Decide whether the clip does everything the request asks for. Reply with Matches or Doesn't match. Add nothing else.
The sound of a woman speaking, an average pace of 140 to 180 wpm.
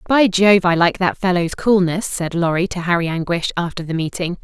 Doesn't match